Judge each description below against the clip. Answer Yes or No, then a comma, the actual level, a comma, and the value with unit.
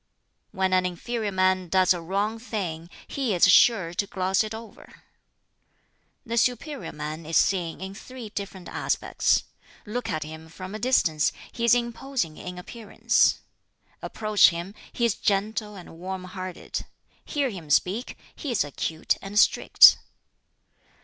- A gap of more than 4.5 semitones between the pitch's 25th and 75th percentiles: No, average, 4.2 semitones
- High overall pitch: Yes, high, 195 Hz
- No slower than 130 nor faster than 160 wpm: Yes, average, 145 wpm